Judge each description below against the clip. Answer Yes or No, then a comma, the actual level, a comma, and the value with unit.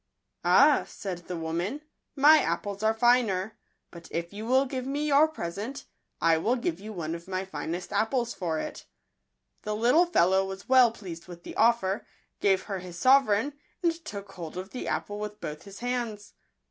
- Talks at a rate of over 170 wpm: Yes, average, 185 wpm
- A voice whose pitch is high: Yes, high, 205 Hz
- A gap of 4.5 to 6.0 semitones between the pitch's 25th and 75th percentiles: Yes, wide, 5.6 semitones